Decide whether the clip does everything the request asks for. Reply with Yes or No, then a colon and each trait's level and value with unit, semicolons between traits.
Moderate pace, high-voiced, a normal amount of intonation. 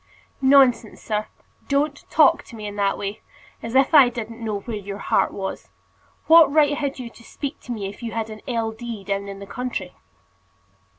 Yes: average, 195 wpm; high, 230 Hz; average, 4.5 semitones